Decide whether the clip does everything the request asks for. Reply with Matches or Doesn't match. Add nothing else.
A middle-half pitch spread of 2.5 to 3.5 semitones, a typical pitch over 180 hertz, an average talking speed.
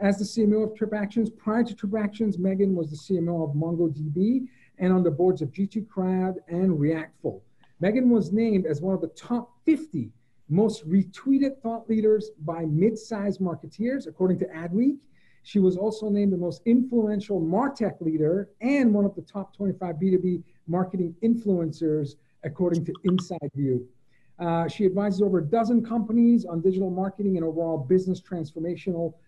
Doesn't match